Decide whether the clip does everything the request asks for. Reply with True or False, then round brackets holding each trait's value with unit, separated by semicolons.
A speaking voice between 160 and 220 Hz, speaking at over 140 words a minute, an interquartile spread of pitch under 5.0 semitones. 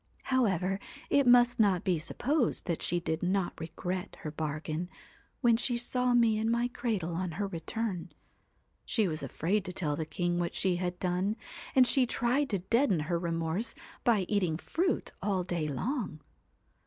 False (190 Hz; 170 wpm; 5.6 semitones)